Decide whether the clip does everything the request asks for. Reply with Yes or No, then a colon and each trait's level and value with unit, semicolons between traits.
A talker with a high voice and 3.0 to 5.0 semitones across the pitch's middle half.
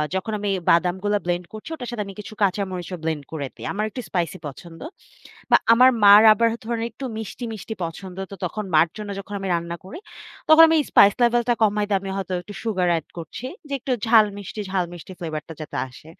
Yes: high, 195 Hz; average, 3.9 semitones